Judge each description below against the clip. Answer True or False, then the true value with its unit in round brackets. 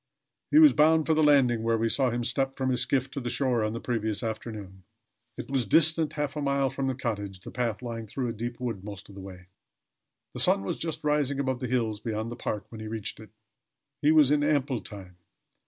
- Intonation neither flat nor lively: True (4.2 semitones)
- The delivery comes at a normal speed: False (235 wpm)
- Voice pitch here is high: False (120 Hz)